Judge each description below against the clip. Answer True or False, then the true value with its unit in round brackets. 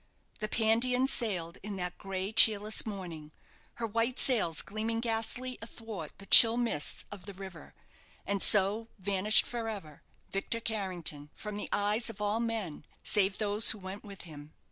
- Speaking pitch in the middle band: False (205 Hz)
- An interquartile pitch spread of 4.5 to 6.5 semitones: False (3.1 semitones)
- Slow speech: False (160 wpm)